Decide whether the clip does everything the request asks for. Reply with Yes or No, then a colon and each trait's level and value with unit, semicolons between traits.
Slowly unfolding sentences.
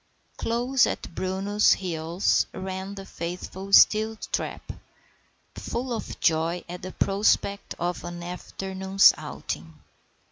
Yes: slow, 105 wpm